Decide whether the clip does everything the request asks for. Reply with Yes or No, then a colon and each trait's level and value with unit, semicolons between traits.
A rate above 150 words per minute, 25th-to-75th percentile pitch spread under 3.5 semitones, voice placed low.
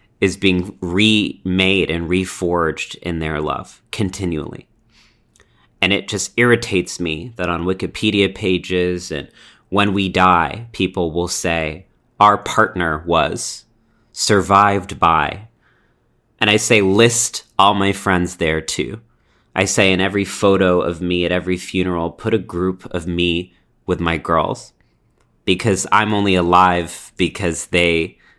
No: slow, 135 wpm; narrow, 2.6 semitones; very low, 95 Hz